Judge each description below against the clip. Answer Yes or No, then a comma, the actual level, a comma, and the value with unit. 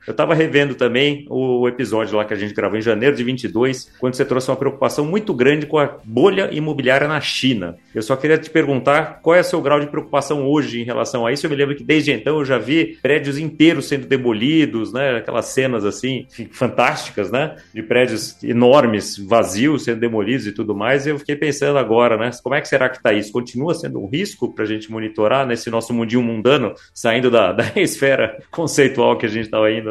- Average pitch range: Yes, average, 4.1 semitones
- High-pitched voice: No, low, 130 Hz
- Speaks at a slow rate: No, fast, 215 wpm